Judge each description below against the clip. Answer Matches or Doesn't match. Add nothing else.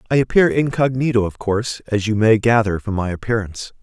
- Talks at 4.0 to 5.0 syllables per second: Doesn't match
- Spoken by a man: Matches